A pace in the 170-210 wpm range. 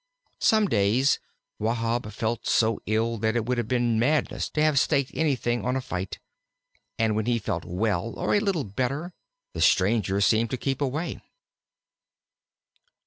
No: average, 155 wpm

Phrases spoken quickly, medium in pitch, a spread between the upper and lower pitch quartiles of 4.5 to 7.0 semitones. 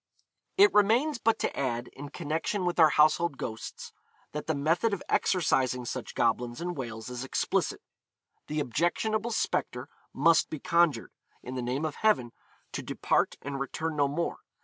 No: average, 160 wpm; medium, 150 Hz; average, 5.3 semitones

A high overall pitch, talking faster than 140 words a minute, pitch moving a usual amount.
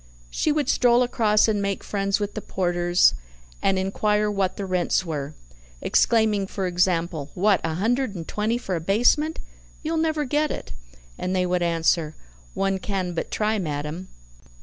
Yes: high, 195 Hz; average, 165 wpm; average, 3.8 semitones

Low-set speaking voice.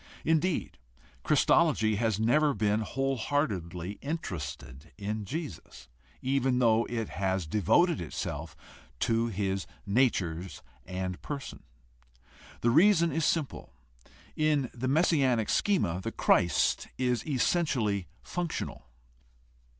Yes: low, 115 Hz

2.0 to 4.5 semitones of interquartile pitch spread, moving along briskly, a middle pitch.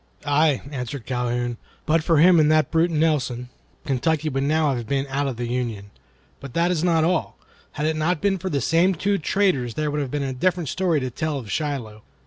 Yes: average, 4.2 semitones; fast, 215 wpm; medium, 150 Hz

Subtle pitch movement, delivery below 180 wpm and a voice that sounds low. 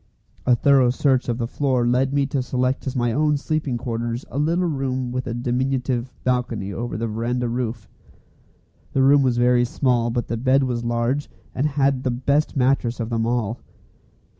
No: narrow, 2.3 semitones; average, 185 wpm; low, 125 Hz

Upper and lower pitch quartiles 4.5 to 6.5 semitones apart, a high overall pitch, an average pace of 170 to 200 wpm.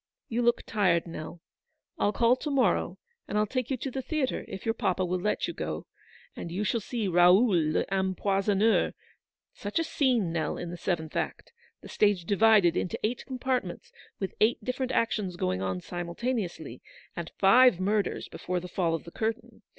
Yes: average, 5.3 semitones; high, 200 Hz; average, 180 wpm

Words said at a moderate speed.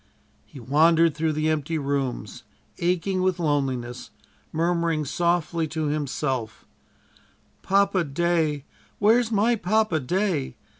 No: slow, 105 wpm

